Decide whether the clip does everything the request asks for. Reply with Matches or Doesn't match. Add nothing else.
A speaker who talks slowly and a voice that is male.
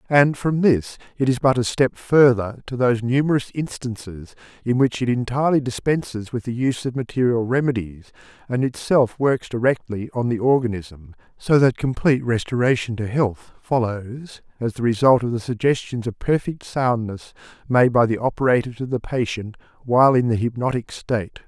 Doesn't match